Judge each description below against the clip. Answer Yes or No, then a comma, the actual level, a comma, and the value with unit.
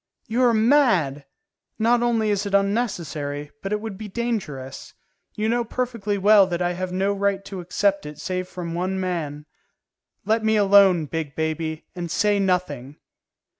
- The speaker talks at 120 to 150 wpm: No, average, 165 wpm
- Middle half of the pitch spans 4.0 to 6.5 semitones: Yes, average, 4.3 semitones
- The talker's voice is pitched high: Yes, high, 195 Hz